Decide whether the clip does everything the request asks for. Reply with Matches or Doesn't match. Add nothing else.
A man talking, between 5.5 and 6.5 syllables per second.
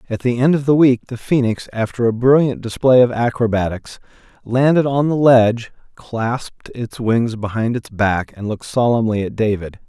Doesn't match